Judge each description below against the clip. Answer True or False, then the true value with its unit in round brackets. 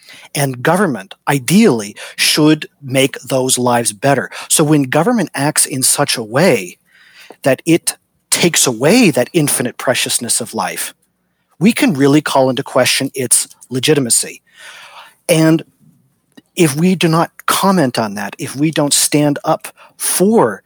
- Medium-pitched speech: True (145 Hz)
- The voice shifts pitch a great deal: False (4.0 semitones)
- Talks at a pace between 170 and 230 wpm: False (135 wpm)